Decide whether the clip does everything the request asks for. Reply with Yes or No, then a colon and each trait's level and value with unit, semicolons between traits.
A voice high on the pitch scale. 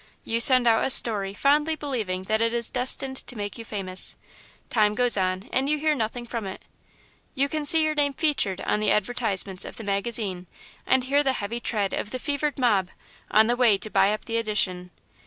Yes: high, 230 Hz